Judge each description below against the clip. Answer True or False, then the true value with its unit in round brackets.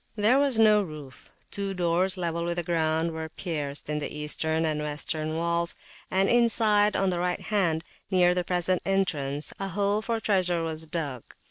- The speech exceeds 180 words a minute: False (175 wpm)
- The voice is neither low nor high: True (175 Hz)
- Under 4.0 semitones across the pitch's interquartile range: True (3.6 semitones)